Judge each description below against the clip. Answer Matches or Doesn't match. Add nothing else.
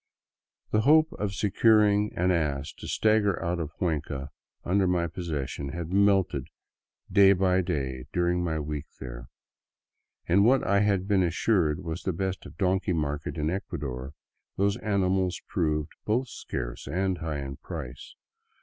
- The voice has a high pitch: Doesn't match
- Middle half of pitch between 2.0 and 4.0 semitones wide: Doesn't match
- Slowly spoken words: Doesn't match